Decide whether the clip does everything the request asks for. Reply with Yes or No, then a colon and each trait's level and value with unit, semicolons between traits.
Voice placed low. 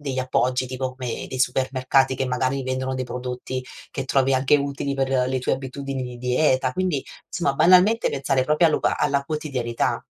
Yes: low, 130 Hz